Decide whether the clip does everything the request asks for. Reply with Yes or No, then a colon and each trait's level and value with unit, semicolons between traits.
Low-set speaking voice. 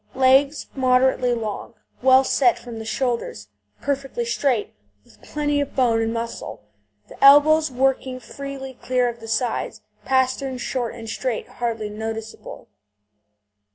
No: very high, 255 Hz